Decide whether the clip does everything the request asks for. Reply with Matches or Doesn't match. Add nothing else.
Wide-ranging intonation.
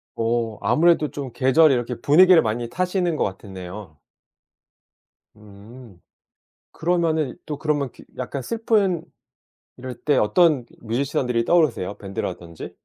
Matches